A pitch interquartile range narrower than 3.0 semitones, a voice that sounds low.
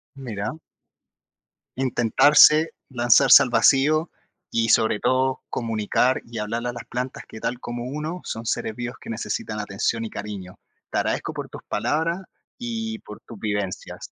No: average, 3.8 semitones; low, 120 Hz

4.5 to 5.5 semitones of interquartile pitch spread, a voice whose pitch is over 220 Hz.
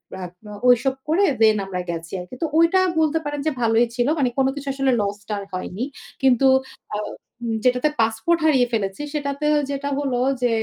Yes: average, 4.8 semitones; very high, 250 Hz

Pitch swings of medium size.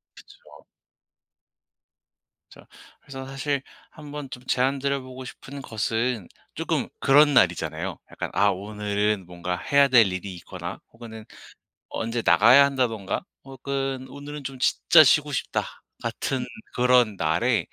Yes: average, 4.7 semitones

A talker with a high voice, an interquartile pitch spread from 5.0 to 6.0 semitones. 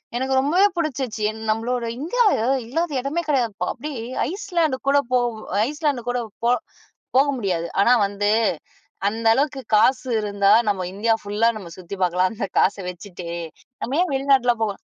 Yes: high, 240 Hz; wide, 5.4 semitones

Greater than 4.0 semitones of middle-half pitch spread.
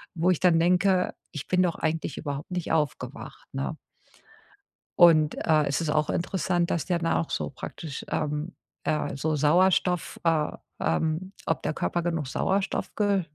No: average, 2.9 semitones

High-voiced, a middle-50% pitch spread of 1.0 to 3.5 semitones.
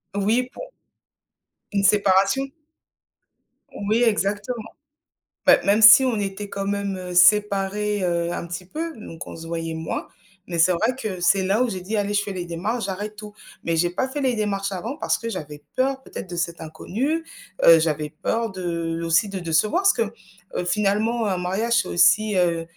No: high, 200 Hz; average, 4.1 semitones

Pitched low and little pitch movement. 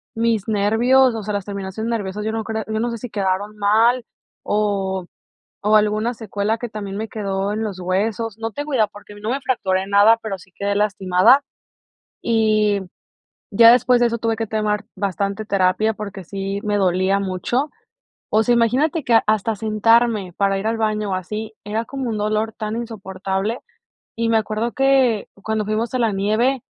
No: high, 215 Hz; narrow, 2.3 semitones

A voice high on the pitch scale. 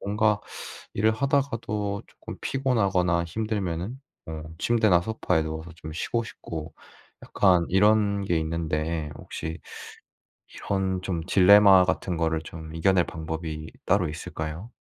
No: very low, 90 Hz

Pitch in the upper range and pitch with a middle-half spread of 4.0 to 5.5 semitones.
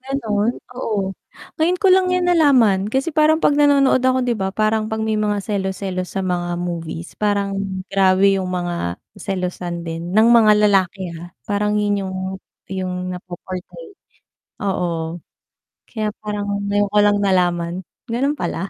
No: high, 200 Hz; average, 3.5 semitones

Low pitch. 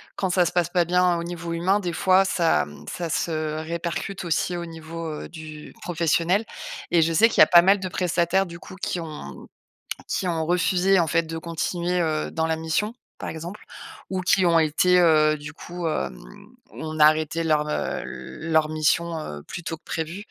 No: medium, 170 Hz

